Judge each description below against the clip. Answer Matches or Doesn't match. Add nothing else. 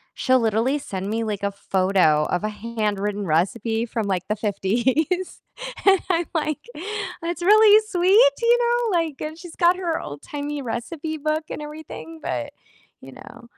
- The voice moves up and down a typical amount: Doesn't match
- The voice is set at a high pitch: Matches